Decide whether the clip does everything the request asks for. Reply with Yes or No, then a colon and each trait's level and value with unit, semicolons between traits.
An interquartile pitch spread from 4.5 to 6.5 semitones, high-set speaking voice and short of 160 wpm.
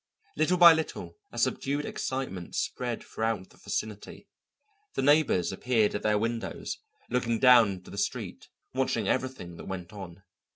No: average, 4.9 semitones; low, 115 Hz; average, 150 wpm